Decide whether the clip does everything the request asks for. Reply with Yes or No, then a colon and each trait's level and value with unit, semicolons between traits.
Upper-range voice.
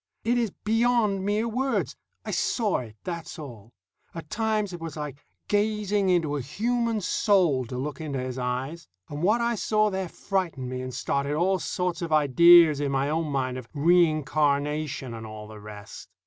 No: medium, 160 Hz